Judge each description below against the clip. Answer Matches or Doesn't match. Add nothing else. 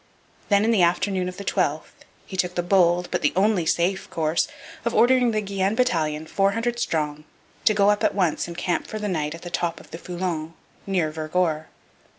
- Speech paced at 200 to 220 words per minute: Matches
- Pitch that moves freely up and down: Doesn't match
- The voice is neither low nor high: Matches